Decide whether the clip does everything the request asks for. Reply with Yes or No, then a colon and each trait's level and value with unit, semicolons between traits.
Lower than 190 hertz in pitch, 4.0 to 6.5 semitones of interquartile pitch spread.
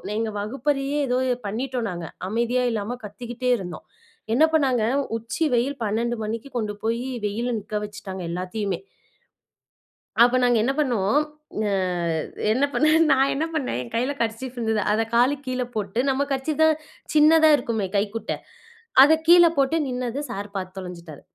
No: high, 235 Hz; average, 4.3 semitones